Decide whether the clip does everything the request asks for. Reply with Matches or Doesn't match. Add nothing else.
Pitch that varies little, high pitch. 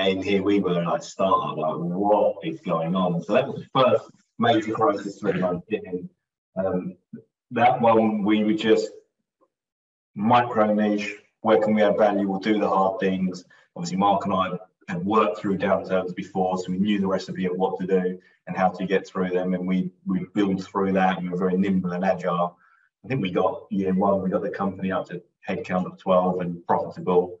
Doesn't match